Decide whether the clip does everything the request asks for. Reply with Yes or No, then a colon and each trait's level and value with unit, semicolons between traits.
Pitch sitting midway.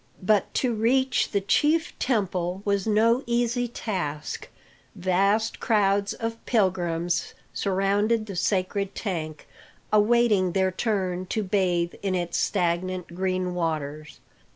No: high, 195 Hz